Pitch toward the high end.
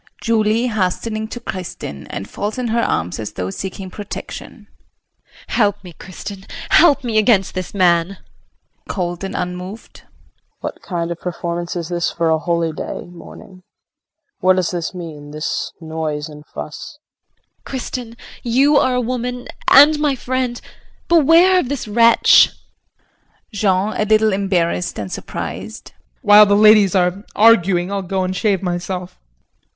Yes: high, 195 Hz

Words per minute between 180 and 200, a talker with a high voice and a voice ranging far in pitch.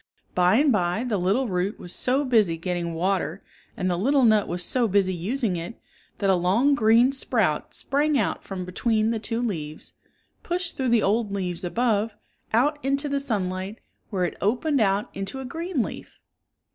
Yes: average, 185 wpm; high, 215 Hz; wide, 5.7 semitones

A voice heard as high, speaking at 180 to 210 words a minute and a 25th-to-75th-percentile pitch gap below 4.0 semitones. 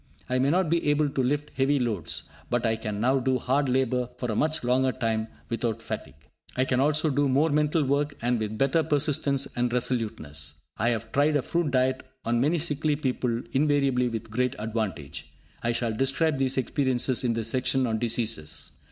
No: low, 130 Hz; average, 190 wpm; average, 3.6 semitones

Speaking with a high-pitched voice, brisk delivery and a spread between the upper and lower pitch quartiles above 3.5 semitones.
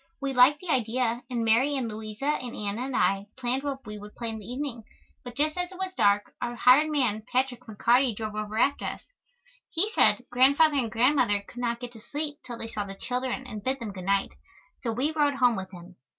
Yes: high, 245 Hz; fast, 225 wpm; average, 4.0 semitones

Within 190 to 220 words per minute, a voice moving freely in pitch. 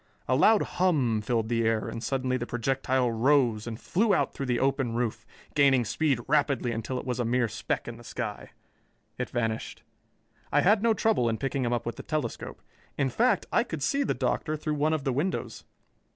No: fast, 205 wpm; average, 4.3 semitones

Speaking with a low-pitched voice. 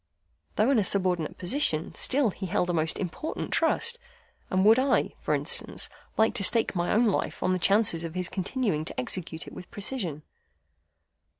No: high, 190 Hz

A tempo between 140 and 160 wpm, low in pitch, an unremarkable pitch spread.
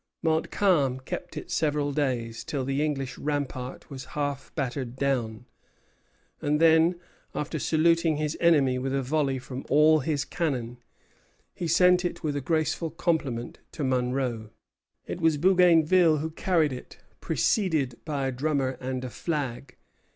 No: average, 145 wpm; medium, 145 Hz; average, 3.6 semitones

